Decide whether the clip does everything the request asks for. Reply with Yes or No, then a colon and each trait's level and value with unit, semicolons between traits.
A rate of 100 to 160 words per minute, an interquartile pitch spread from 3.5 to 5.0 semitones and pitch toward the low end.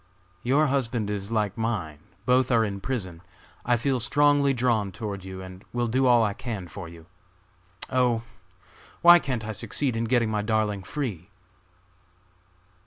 Yes: average, 155 wpm; average, 4.2 semitones; low, 115 Hz